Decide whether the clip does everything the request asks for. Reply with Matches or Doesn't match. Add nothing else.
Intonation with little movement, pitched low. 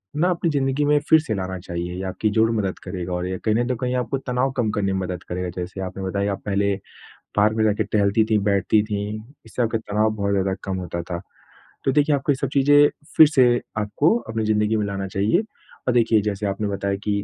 Doesn't match